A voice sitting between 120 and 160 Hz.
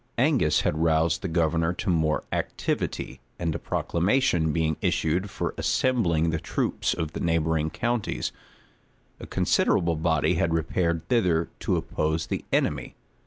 No: very low, 80 Hz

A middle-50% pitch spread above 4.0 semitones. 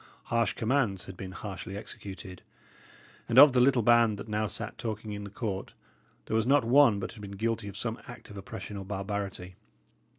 No: average, 2.9 semitones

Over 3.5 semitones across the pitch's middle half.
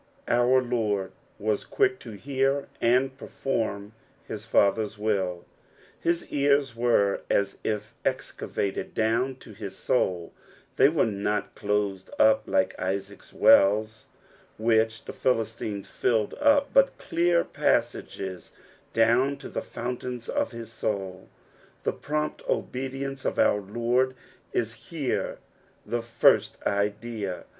Yes: average, 4.2 semitones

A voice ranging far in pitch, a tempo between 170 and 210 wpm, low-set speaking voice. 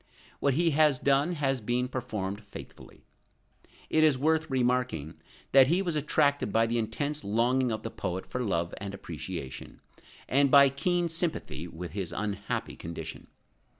No: wide, 6.3 semitones; average, 150 wpm; low, 125 Hz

